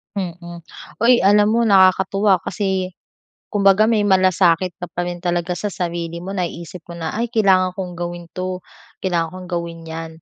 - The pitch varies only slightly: Yes, narrow, 2.2 semitones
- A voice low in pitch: No, medium, 185 Hz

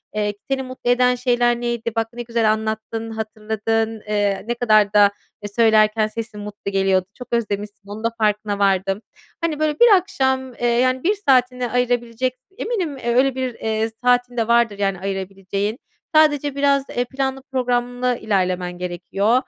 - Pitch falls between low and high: No, high, 230 Hz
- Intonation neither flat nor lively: Yes, average, 3.3 semitones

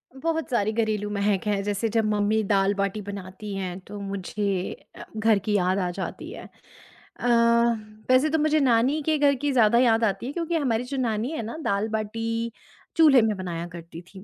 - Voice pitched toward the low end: No, high, 215 Hz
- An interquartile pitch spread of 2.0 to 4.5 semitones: Yes, average, 3.9 semitones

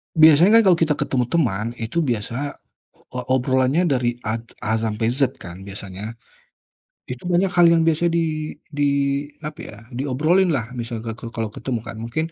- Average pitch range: No, wide, 5.9 semitones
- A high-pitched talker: No, low, 130 Hz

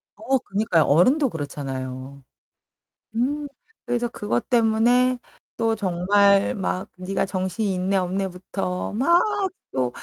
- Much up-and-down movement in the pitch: No, average, 4.6 semitones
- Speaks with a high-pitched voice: Yes, high, 195 Hz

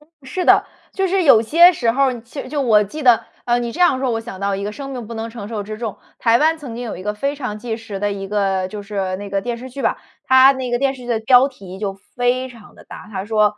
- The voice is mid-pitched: No, high, 235 Hz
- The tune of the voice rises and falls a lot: No, average, 4.0 semitones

